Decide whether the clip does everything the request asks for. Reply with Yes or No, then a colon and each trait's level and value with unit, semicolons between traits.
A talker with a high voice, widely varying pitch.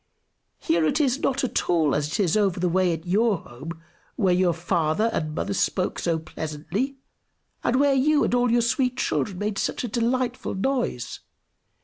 Yes: high, 195 Hz; wide, 6.9 semitones